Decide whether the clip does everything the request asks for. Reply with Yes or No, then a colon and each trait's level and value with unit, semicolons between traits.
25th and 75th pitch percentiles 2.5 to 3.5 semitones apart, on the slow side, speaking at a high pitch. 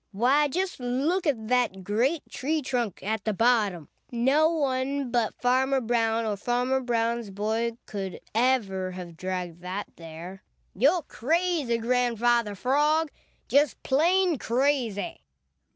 No: average, 4.8 semitones; slow, 125 wpm; high, 240 Hz